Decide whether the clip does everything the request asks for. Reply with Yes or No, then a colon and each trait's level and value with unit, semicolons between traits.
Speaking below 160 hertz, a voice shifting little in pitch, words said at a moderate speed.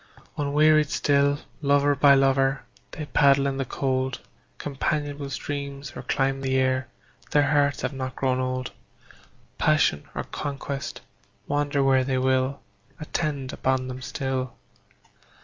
No: low, 135 Hz; narrow, 1.5 semitones; slow, 130 wpm